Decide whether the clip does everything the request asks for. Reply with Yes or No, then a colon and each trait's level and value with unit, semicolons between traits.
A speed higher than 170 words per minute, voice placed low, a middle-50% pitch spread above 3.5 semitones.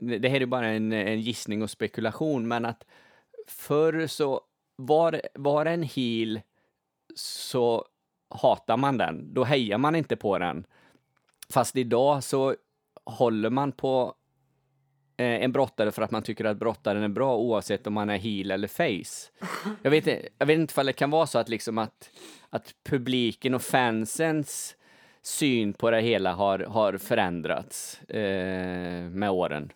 No: average, 155 wpm; low, 125 Hz; average, 4.1 semitones